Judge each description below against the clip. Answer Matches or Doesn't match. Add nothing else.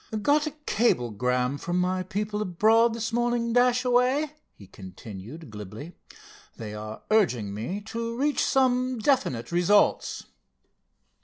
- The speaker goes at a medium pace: Doesn't match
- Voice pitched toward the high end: Matches